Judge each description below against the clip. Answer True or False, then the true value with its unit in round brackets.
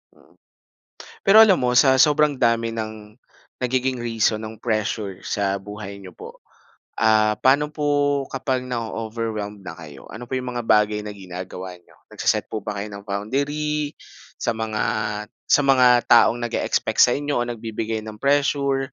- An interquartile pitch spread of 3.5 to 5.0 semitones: True (4.0 semitones)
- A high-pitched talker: False (115 Hz)